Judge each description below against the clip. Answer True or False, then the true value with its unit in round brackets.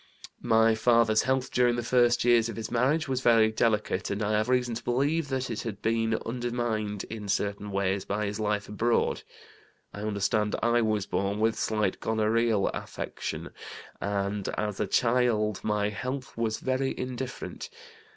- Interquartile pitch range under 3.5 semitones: True (2.5 semitones)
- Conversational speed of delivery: True (160 wpm)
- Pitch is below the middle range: True (110 Hz)